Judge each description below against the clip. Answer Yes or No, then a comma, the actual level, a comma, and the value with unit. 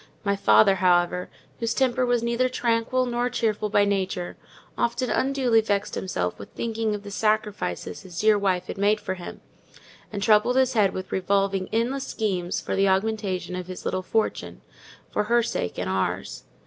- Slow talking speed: No, average, 175 wpm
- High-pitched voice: Yes, high, 205 Hz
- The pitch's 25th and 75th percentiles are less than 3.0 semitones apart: No, average, 3.7 semitones